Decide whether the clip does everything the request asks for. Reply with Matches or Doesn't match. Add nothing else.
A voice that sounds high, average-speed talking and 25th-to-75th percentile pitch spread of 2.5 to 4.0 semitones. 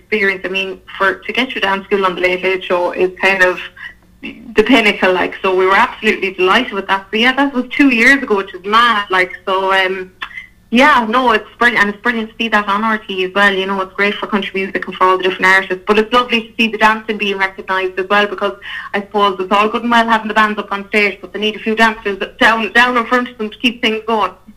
Doesn't match